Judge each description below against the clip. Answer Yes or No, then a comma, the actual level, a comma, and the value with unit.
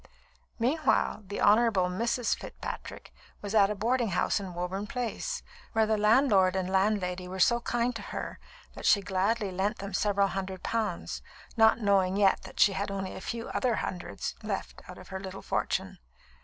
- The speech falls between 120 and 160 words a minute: No, average, 175 wpm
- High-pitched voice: Yes, high, 200 Hz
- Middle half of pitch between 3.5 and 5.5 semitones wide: No, average, 3.0 semitones